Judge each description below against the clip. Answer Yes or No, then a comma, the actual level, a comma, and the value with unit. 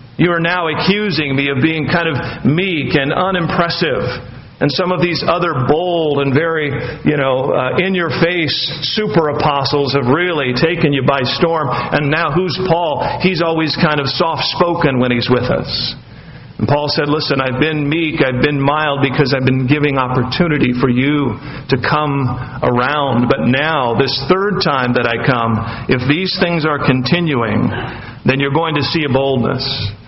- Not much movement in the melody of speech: No, average, 4.0 semitones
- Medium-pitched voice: Yes, medium, 145 Hz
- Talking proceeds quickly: No, average, 175 wpm